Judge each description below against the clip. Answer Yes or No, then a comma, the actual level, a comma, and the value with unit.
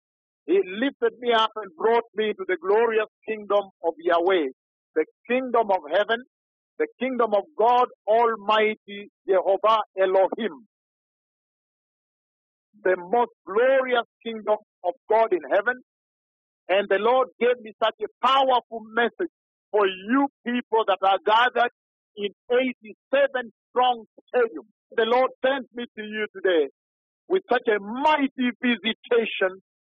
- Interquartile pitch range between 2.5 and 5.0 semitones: Yes, average, 3.4 semitones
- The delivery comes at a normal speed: No, slow, 125 wpm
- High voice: Yes, high, 230 Hz